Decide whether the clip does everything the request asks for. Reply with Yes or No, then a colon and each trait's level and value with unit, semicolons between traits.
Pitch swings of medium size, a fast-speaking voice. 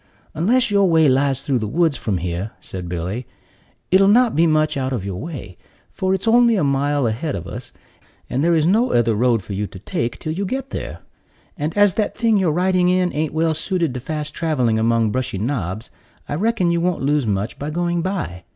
No: wide, 7.6 semitones; fast, 215 wpm